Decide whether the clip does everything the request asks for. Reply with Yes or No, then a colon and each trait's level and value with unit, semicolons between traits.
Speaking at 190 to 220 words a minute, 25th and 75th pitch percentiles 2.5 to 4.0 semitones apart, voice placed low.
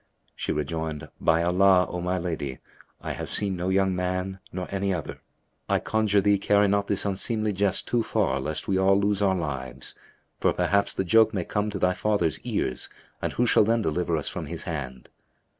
Yes: average, 195 wpm; average, 3.6 semitones; very low, 95 Hz